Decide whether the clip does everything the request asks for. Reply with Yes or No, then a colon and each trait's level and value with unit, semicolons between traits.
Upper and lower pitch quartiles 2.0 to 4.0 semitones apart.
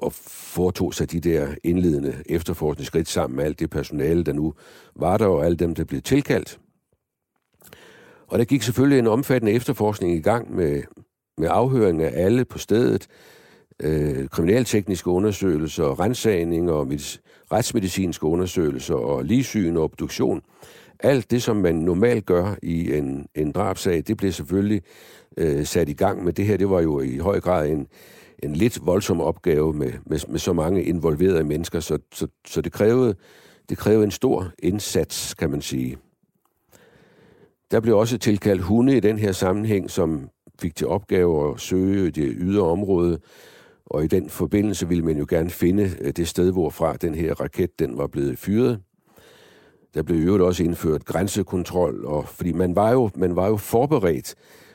No: average, 4.4 semitones